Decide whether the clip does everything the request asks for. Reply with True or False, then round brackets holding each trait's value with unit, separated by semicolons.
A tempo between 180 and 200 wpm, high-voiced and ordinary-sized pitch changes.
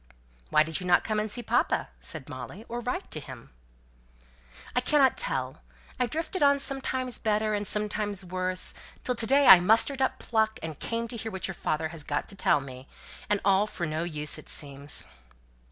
False (195 wpm; 205 Hz; 7.1 semitones)